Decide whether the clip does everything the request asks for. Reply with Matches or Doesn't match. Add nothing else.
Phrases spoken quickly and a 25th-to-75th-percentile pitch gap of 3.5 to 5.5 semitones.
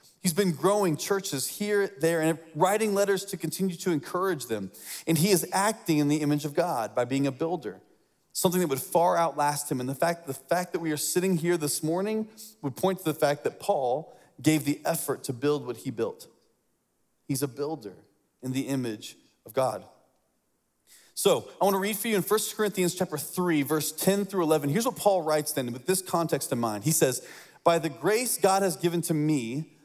Matches